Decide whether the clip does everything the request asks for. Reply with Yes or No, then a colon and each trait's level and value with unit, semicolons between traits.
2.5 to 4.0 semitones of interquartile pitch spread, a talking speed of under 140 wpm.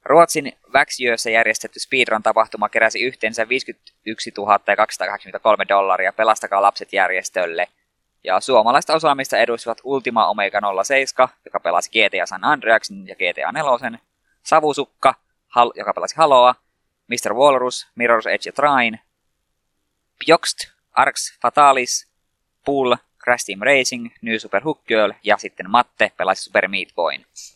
Yes: average, 3.6 semitones; average, 125 wpm